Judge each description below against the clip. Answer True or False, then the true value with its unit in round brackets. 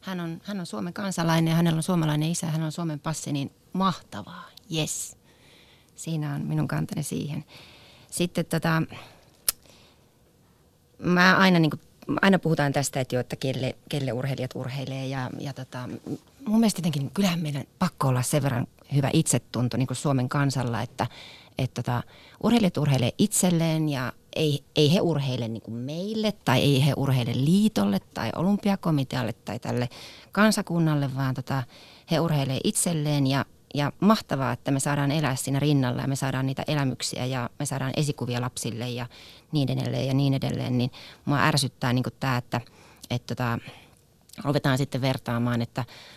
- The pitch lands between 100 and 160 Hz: True (140 Hz)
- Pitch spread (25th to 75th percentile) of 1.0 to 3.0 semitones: False (4.3 semitones)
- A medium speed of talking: False (160 wpm)